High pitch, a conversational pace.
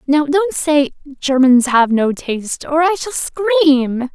Yes: very high, 295 Hz; average, 160 wpm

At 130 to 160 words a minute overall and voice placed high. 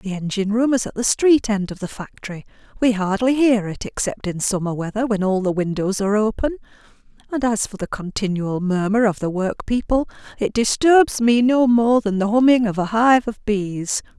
No: fast, 205 wpm; high, 215 Hz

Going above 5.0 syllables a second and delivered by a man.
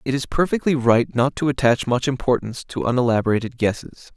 Yes: 6.0 syllables/s; male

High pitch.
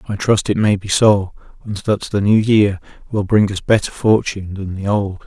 No: low, 100 Hz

